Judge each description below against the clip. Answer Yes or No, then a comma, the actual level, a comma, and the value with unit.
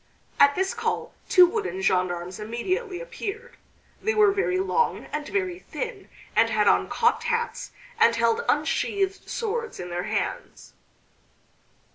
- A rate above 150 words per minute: No, slow, 135 wpm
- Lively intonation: Yes, wide, 8.1 semitones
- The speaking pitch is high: Yes, very high, 390 Hz